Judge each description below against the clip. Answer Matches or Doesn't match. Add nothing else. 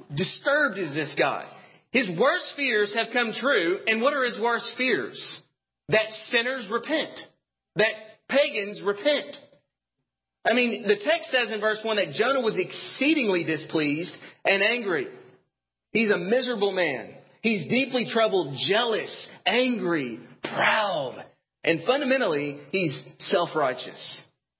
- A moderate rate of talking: Doesn't match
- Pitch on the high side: Matches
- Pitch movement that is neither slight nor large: Matches